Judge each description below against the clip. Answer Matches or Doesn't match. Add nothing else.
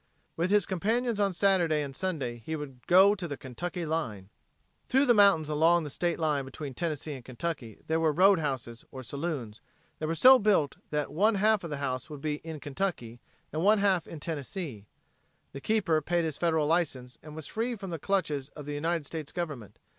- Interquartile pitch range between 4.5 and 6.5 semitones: Matches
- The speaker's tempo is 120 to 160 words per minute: Doesn't match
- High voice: Doesn't match